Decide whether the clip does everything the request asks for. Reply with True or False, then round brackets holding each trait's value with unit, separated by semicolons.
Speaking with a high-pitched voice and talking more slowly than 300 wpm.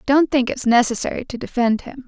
True (255 Hz; 200 wpm)